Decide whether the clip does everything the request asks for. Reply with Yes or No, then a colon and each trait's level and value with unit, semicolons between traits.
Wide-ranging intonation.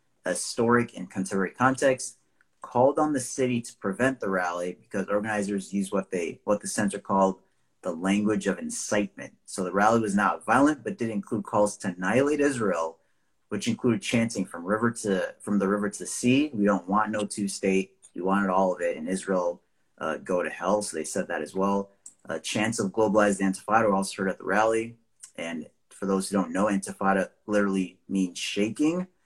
No: average, 3.3 semitones